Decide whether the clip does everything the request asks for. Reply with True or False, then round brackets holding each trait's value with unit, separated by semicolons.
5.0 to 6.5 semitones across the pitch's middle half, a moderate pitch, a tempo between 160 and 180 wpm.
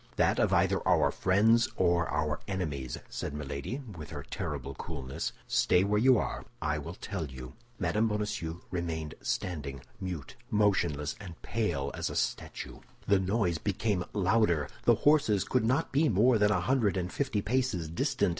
False (5.5 semitones; 95 Hz; 165 wpm)